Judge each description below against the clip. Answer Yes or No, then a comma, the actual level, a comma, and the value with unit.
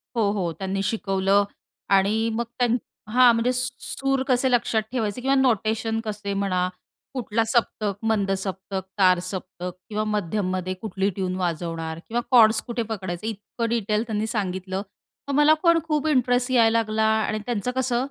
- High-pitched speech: Yes, high, 215 Hz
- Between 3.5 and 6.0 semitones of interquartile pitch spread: Yes, average, 3.8 semitones